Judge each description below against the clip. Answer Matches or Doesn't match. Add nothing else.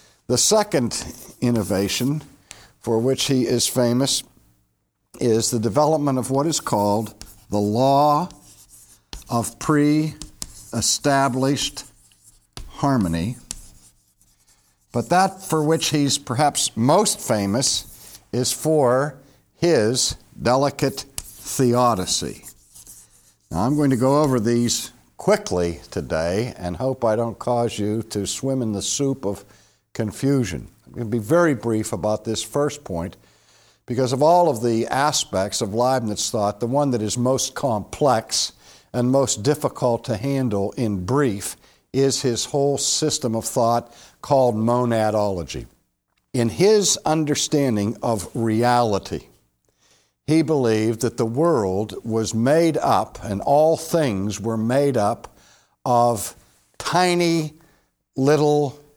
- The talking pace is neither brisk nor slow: Doesn't match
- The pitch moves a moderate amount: Matches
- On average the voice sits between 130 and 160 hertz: Doesn't match